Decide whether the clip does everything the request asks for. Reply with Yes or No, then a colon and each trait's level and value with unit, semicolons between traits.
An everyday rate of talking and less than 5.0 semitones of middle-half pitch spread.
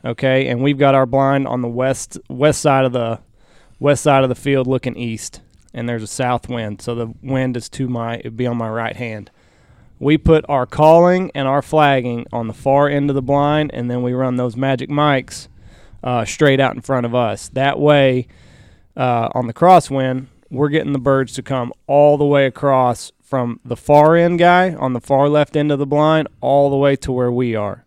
No: fast, 215 wpm; average, 2.8 semitones